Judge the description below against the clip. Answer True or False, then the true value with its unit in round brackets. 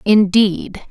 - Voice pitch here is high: True (200 Hz)